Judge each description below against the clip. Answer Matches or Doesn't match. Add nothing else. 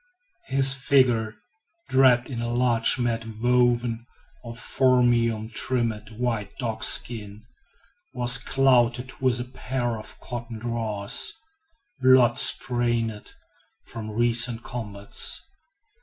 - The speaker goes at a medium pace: Doesn't match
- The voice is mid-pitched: Doesn't match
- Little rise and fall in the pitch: Matches